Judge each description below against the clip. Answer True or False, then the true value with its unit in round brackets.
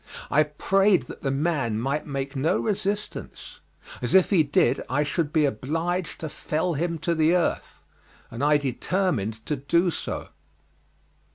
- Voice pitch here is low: False (155 Hz)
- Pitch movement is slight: False (4.1 semitones)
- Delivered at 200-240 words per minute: False (155 wpm)